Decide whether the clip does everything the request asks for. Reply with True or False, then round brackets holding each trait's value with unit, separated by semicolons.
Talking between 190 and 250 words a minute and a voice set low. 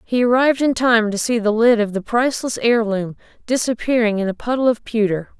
False (200 wpm; 230 Hz)